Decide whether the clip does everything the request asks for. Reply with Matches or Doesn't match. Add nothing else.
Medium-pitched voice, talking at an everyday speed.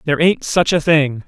Doesn't match